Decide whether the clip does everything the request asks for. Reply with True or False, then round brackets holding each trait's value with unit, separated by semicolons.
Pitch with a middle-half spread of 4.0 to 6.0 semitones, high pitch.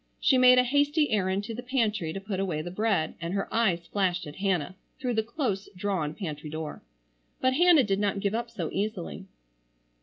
True (4.9 semitones; 200 Hz)